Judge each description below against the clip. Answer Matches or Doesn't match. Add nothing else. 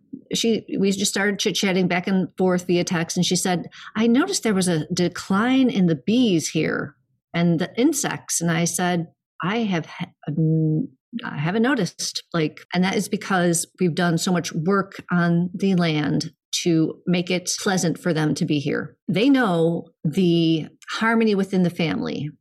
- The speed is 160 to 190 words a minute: Matches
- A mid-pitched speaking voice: Matches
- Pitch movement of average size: Matches